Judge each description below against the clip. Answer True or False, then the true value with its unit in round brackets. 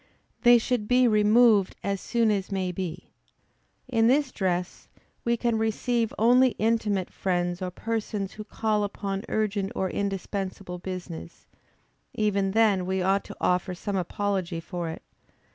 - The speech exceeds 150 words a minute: False (145 wpm)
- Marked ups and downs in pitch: False (3.3 semitones)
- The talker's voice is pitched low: False (200 Hz)